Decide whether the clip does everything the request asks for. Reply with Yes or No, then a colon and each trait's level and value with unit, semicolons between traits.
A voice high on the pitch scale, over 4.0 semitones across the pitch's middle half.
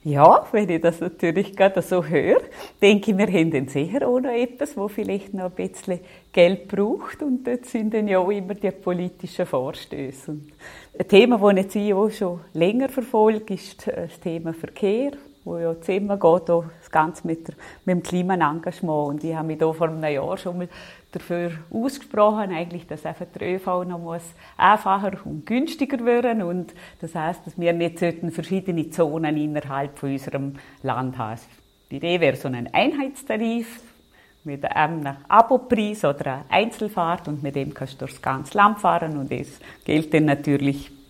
No: medium, 175 Hz; average, 4.7 semitones